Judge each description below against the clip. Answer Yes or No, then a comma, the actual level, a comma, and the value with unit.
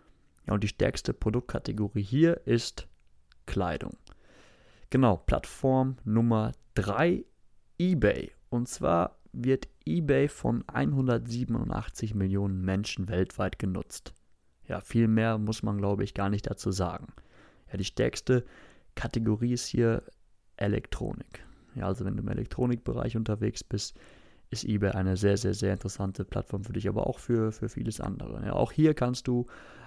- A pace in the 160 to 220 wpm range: No, average, 140 wpm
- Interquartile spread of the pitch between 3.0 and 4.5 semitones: Yes, average, 3.5 semitones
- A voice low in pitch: Yes, low, 110 Hz